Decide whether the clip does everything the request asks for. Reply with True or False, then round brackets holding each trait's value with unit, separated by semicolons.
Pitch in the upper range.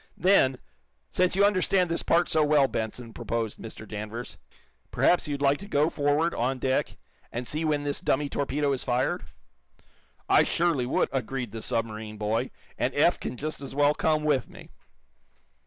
False (140 Hz)